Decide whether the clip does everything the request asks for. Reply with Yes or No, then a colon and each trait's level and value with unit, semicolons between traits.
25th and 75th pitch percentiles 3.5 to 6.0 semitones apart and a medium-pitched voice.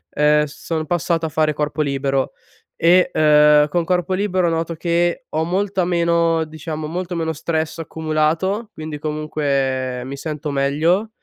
No: narrow, 2.4 semitones; medium, 160 Hz